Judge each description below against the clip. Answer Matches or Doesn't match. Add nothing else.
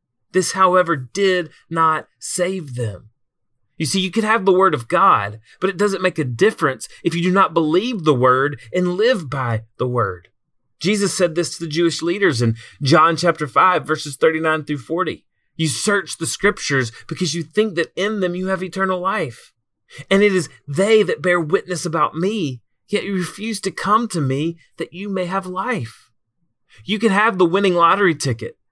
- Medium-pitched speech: Matches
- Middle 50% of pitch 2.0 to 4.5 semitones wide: Doesn't match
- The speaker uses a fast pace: Doesn't match